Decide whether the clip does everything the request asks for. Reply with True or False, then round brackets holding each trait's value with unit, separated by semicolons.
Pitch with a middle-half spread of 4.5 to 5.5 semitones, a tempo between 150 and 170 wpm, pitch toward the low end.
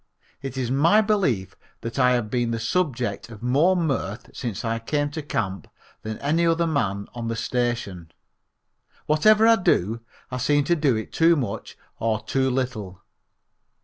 True (5.2 semitones; 165 wpm; 125 Hz)